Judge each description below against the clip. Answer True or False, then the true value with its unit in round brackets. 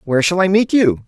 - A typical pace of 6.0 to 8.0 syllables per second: True (6.3 syllables/s)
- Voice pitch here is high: False (170 Hz)